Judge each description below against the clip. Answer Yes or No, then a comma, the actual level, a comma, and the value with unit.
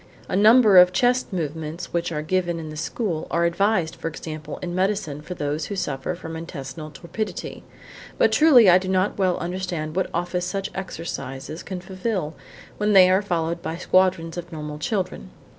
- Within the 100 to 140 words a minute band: No, average, 175 wpm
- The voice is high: No, medium, 175 Hz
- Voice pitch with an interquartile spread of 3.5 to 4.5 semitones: No, average, 3.0 semitones